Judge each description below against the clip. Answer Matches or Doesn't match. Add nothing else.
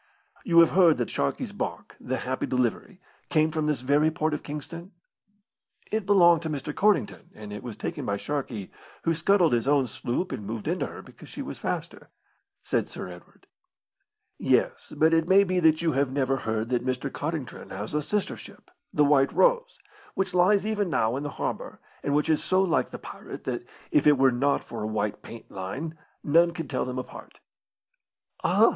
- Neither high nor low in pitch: Matches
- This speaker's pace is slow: Doesn't match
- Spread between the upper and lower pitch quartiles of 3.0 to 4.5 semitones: Doesn't match